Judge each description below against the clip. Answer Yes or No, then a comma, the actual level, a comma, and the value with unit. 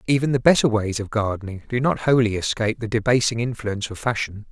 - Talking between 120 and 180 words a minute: No, average, 200 wpm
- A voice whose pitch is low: Yes, low, 115 Hz